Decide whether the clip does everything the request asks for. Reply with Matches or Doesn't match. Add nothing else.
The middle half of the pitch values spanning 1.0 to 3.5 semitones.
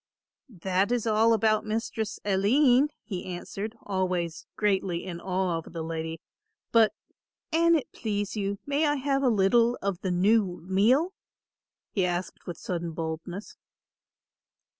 Doesn't match